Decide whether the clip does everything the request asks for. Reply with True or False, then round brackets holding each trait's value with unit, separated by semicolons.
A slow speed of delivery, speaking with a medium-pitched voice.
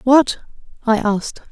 False (120 wpm; 235 Hz)